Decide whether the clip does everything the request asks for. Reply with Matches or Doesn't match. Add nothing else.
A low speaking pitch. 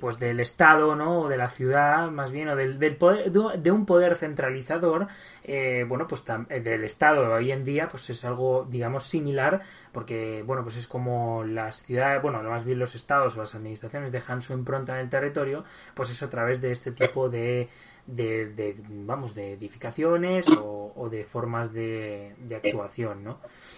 Matches